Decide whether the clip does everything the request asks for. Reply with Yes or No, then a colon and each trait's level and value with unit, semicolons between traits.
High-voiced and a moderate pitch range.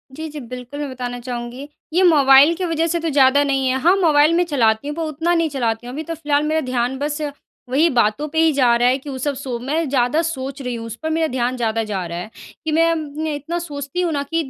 Yes: very high, 285 Hz; average, 4.2 semitones